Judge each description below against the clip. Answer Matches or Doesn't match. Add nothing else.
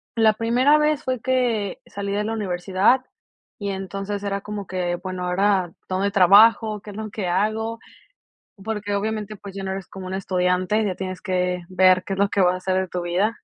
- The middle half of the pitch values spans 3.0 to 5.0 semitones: Doesn't match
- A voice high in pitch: Matches